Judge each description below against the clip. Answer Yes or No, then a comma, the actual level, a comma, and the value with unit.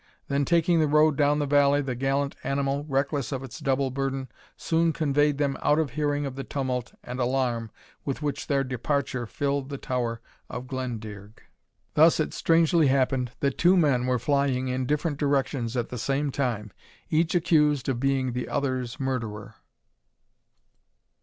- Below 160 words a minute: No, average, 165 wpm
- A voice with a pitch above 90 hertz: Yes, low, 135 Hz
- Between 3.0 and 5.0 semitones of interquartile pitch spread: No, narrow, 2.4 semitones